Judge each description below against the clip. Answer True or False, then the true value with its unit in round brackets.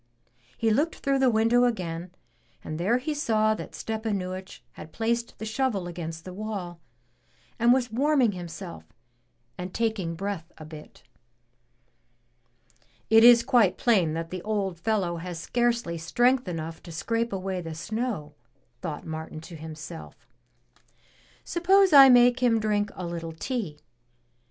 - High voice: True (205 Hz)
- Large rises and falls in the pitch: True (5.8 semitones)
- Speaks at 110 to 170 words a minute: True (140 wpm)